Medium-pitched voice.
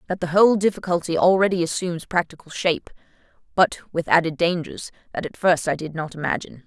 Yes: medium, 170 Hz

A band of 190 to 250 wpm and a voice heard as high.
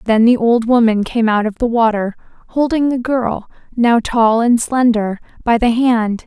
No: average, 180 wpm; high, 230 Hz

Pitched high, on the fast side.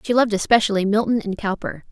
No: high, 210 Hz; average, 190 wpm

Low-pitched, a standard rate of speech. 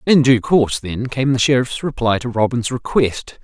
Yes: low, 125 Hz; average, 190 wpm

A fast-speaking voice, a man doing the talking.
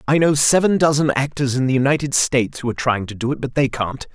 Yes: fast, 260 wpm; male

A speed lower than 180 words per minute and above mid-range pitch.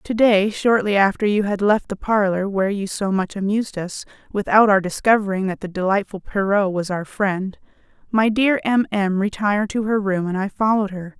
No: average, 200 wpm; high, 200 Hz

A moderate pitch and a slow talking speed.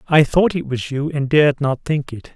No: medium, 145 Hz; fast, 255 wpm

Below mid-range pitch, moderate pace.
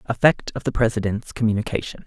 Yes: low, 110 Hz; average, 145 wpm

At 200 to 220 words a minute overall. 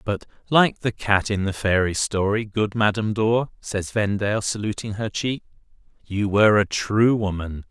No: average, 165 wpm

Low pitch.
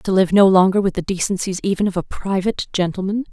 No: high, 190 Hz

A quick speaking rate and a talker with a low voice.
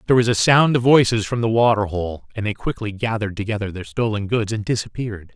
Yes: fast, 225 wpm; low, 110 Hz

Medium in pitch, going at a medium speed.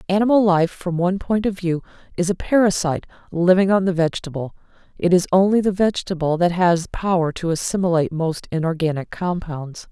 Yes: medium, 180 Hz; average, 165 wpm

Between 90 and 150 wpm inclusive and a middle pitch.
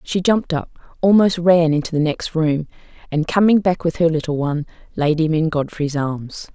No: average, 195 wpm; medium, 160 Hz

